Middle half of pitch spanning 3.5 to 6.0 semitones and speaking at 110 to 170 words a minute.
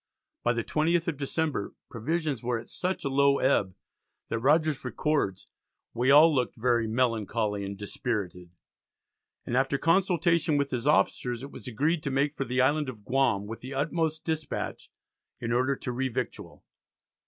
Yes: average, 4.6 semitones; average, 160 wpm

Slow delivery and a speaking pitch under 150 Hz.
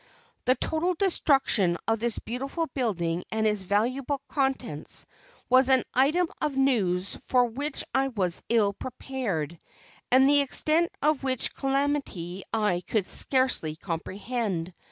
No: slow, 130 wpm; very high, 250 Hz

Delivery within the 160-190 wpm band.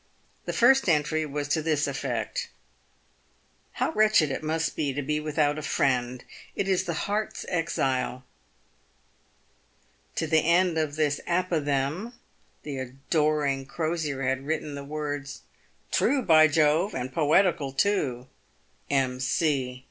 No: average, 140 wpm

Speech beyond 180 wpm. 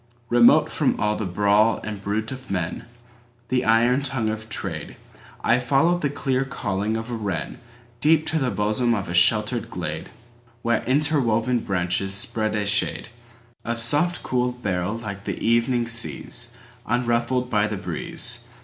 No: slow, 135 wpm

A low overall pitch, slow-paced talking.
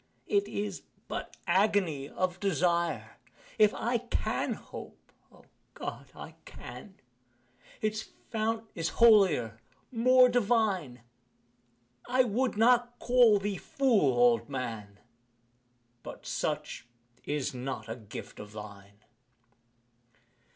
No: high, 190 Hz; slow, 105 wpm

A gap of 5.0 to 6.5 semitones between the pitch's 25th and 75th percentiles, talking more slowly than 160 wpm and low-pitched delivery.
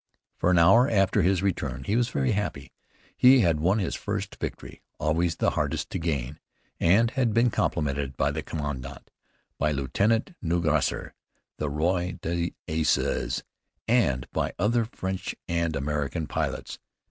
Yes: wide, 5.4 semitones; average, 145 wpm; very low, 85 Hz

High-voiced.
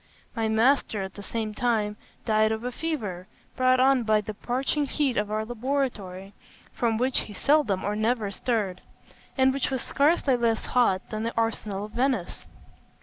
Yes: high, 225 Hz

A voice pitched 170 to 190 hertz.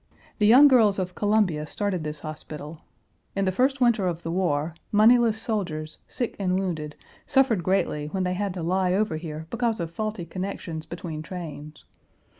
Yes: medium, 185 Hz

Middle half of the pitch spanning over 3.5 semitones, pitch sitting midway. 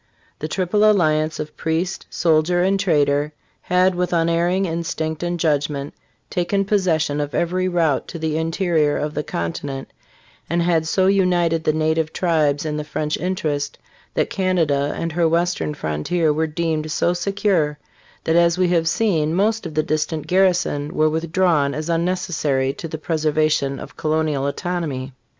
No: average, 2.7 semitones; medium, 160 Hz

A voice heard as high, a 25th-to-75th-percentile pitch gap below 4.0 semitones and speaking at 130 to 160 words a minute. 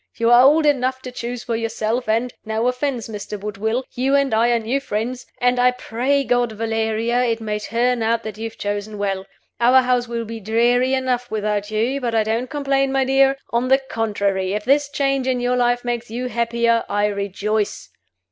No: high, 235 Hz; narrow, 2.5 semitones; average, 200 wpm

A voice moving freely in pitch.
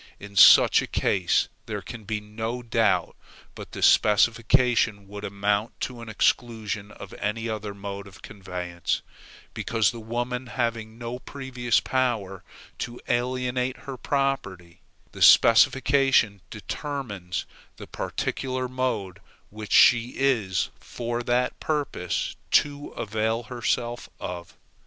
No: average, 3.6 semitones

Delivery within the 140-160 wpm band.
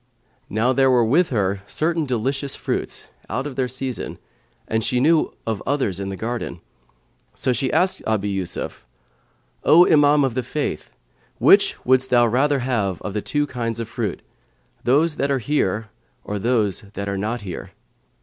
No: average, 170 wpm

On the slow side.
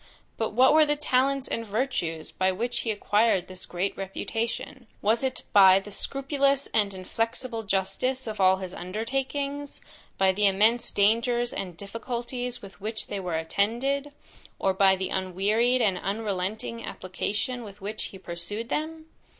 No: average, 150 wpm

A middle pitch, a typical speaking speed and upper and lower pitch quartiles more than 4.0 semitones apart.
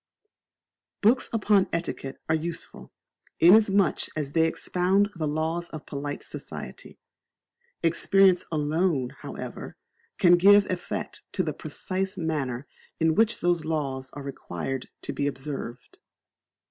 No: medium, 165 Hz; slow, 120 wpm; average, 4.5 semitones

